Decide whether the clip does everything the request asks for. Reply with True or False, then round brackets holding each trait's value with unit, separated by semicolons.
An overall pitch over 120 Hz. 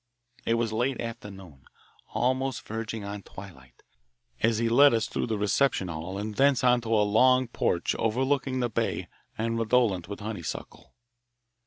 False (115 Hz)